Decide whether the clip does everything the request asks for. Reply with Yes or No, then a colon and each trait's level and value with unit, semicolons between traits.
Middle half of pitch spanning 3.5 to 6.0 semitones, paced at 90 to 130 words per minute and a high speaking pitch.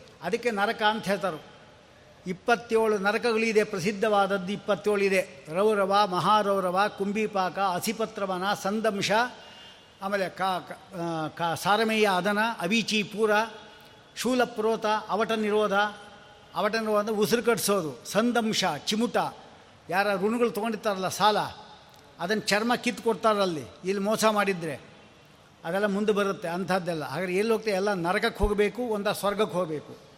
No: narrow, 2.4 semitones; average, 100 wpm; high, 205 Hz